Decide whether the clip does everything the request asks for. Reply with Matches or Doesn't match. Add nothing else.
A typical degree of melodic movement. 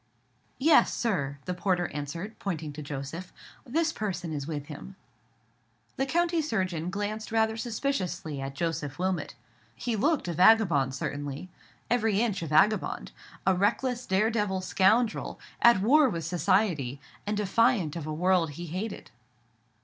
Doesn't match